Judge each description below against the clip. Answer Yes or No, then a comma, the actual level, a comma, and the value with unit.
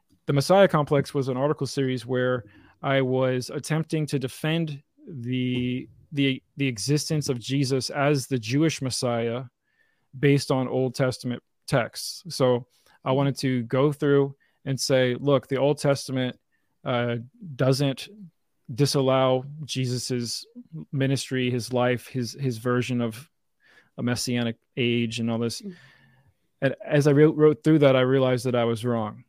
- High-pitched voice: No, low, 135 Hz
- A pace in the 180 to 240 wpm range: No, average, 145 wpm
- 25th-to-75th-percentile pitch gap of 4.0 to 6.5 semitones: No, narrow, 2.4 semitones